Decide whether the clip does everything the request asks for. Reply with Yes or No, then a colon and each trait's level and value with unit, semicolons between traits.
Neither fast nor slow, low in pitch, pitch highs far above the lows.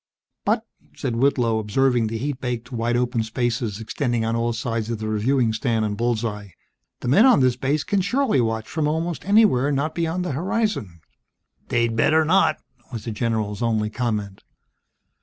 No: average, 175 wpm; low, 120 Hz; average, 4.4 semitones